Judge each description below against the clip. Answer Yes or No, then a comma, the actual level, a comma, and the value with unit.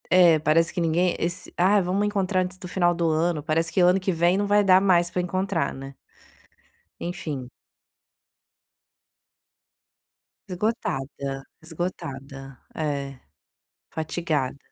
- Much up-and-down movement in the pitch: No, average, 3.2 semitones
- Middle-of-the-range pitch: Yes, medium, 170 Hz